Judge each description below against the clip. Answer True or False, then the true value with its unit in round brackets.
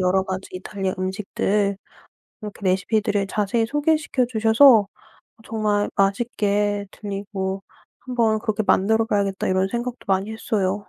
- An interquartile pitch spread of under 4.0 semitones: True (2.5 semitones)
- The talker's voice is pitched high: True (205 Hz)